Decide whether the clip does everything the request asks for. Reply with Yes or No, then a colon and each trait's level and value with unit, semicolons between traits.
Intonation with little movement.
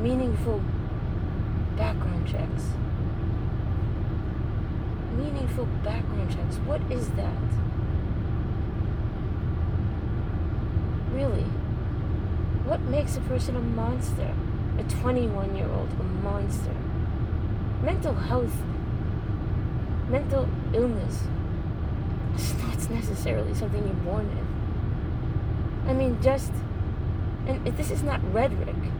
Yes: narrow, 2.3 semitones